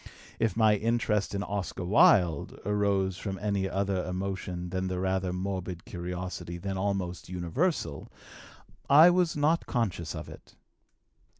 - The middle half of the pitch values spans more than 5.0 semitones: No, narrow, 2.5 semitones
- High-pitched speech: No, very low, 95 Hz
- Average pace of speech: No, slow, 130 wpm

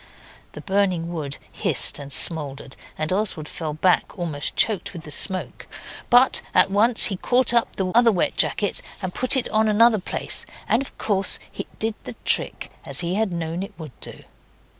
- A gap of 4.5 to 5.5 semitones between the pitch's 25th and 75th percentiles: Yes, average, 5.0 semitones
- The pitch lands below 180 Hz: No, high, 190 Hz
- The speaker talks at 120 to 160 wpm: No, average, 180 wpm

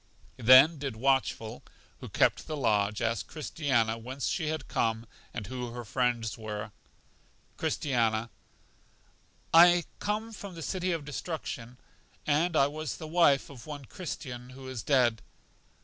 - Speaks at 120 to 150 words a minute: Yes, average, 140 wpm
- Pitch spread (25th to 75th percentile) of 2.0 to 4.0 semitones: No, average, 5.2 semitones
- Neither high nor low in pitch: No, low, 130 Hz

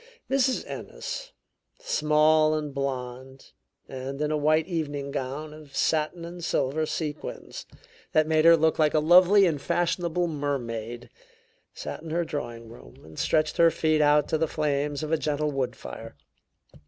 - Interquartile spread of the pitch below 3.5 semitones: Yes, narrow, 2.6 semitones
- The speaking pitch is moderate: Yes, medium, 150 Hz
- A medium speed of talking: Yes, average, 155 wpm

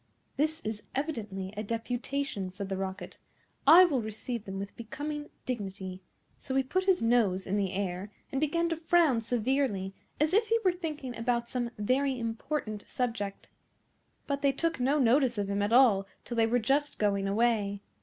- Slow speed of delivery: No, average, 175 wpm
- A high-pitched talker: Yes, high, 235 Hz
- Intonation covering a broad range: Yes, wide, 5.7 semitones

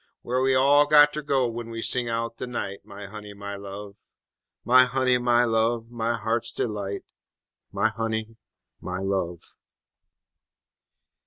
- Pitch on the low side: Yes, low, 115 Hz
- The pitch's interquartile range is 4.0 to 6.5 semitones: No, average, 3.5 semitones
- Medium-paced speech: Yes, average, 145 wpm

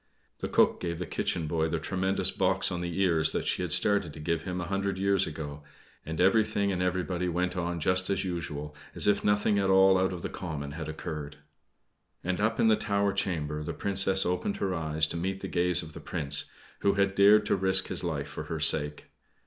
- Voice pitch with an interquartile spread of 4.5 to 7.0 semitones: No, average, 3.3 semitones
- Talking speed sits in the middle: No, fast, 220 wpm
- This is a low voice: Yes, very low, 90 Hz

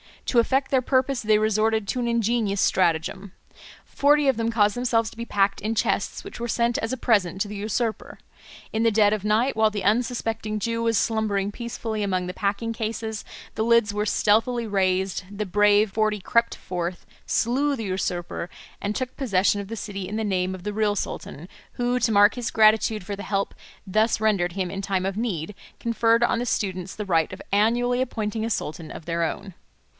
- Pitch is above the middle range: Yes, high, 215 Hz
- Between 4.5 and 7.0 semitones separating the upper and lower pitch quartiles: No, average, 2.7 semitones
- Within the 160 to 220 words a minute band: Yes, average, 200 wpm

